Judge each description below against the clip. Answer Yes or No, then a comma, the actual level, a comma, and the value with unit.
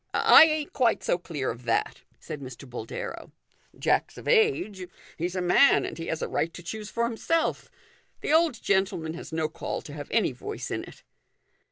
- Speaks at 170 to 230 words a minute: Yes, average, 195 wpm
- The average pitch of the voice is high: No, medium, 180 Hz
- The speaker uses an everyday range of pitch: No, wide, 7.2 semitones